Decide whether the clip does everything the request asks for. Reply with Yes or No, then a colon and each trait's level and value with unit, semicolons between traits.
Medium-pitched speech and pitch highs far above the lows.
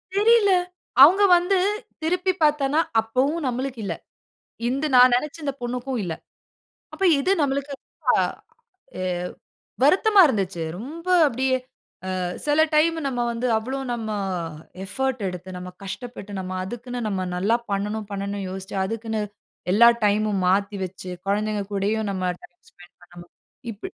No: high, 235 Hz; wide, 5.9 semitones